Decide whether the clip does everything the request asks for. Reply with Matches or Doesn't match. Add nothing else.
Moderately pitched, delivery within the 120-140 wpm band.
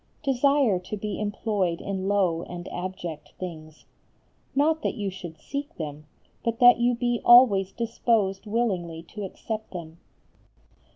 Doesn't match